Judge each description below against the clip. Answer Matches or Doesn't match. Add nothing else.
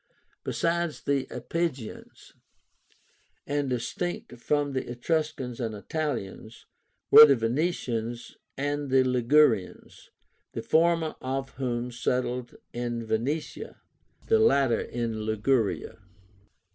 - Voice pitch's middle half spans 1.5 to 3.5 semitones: Doesn't match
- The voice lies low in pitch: Matches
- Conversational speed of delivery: Doesn't match